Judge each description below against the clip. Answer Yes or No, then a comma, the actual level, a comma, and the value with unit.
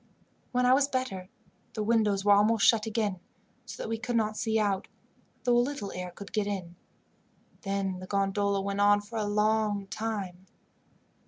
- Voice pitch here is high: Yes, high, 205 Hz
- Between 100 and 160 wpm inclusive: No, average, 175 wpm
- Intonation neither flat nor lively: No, narrow, 2.2 semitones